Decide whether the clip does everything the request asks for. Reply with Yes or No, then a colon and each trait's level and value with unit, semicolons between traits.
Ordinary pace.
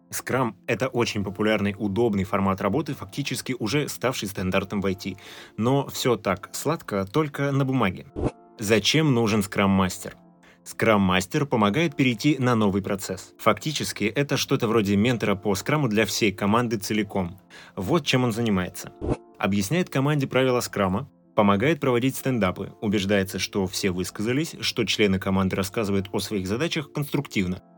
Yes: average, 140 wpm